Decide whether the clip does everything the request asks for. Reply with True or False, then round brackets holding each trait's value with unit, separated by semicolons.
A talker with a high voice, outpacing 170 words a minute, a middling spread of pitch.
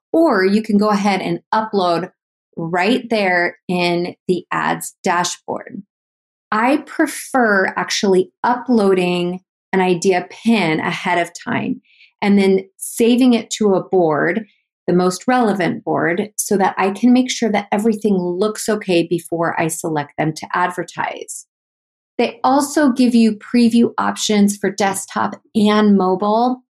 False (200 Hz; 135 wpm; 4.3 semitones)